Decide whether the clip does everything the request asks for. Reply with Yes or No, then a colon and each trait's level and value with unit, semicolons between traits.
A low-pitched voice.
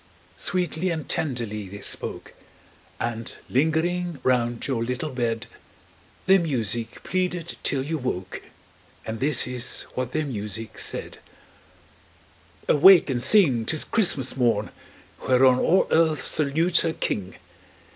Yes: low, 130 Hz